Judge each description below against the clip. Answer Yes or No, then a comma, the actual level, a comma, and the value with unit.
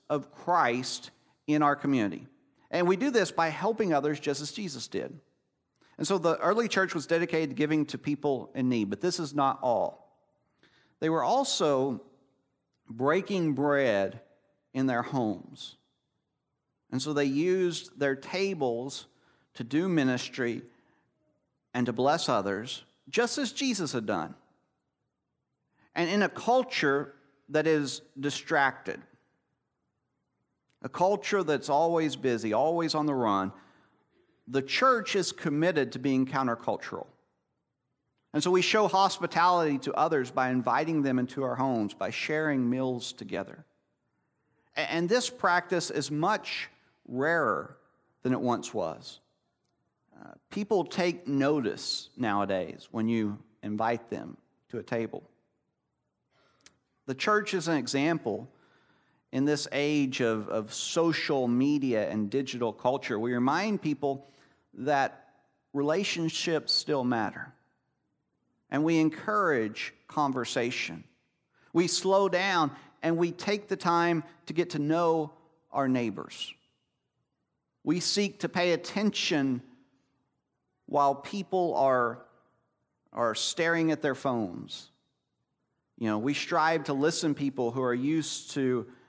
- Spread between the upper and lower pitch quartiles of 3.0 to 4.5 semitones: No, average, 4.9 semitones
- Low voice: No, medium, 145 Hz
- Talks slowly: Yes, slow, 125 wpm